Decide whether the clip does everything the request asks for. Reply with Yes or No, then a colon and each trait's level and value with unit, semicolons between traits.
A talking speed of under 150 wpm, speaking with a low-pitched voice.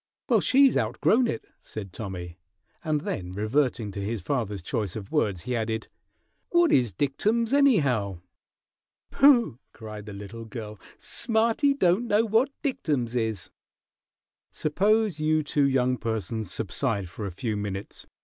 Yes: average, 140 wpm; low, 120 Hz